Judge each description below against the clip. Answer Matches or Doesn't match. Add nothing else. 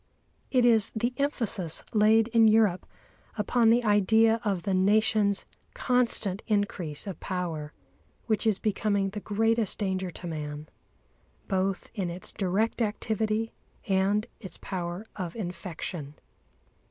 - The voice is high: Matches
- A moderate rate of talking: Doesn't match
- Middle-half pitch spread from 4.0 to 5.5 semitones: Doesn't match